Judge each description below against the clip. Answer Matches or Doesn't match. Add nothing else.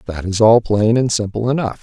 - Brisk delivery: Matches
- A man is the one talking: Matches